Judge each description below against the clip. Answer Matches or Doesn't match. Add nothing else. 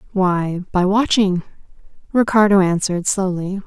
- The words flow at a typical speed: Doesn't match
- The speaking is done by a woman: Matches